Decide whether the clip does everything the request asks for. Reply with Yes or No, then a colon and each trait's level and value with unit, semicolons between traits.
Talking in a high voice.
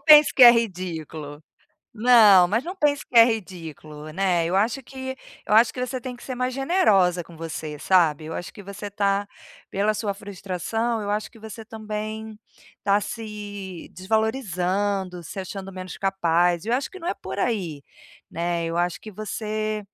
Yes: high, 205 Hz